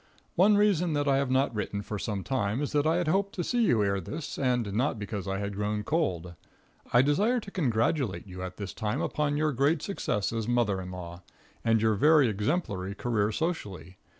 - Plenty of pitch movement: Yes, wide, 7.0 semitones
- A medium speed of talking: No, fast, 210 wpm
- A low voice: Yes, low, 115 Hz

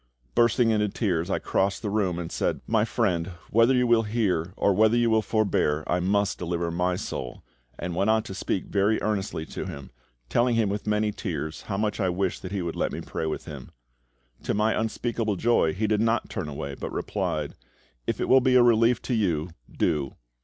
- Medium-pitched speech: No, low, 105 Hz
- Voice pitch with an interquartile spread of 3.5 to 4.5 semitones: Yes, average, 4.2 semitones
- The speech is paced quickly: Yes, fast, 210 wpm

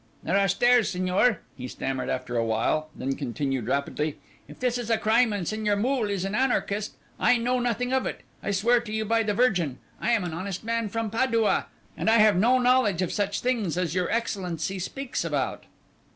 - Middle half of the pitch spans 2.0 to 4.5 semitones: No, average, 5.1 semitones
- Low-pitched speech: No, high, 210 Hz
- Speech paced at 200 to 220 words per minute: Yes, fast, 205 wpm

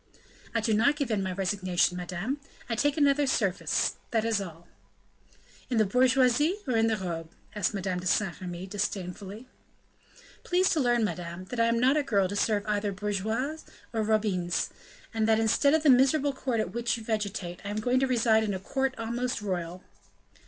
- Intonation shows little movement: No, average, 4.7 semitones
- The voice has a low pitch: No, high, 220 Hz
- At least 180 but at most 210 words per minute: Yes, average, 190 wpm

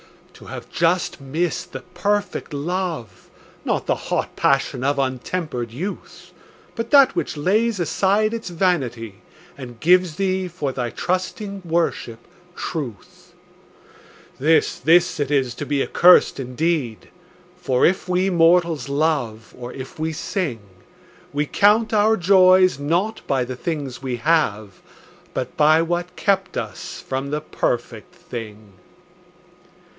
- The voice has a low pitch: No, medium, 160 Hz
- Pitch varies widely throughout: Yes, wide, 5.9 semitones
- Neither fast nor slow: No, slow, 130 wpm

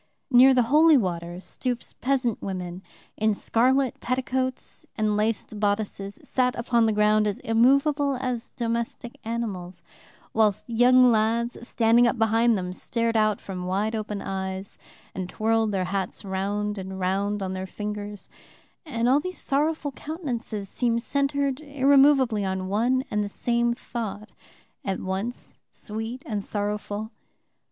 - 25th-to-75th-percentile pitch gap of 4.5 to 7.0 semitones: No, average, 3.7 semitones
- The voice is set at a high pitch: Yes, high, 225 Hz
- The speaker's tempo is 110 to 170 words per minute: Yes, average, 140 wpm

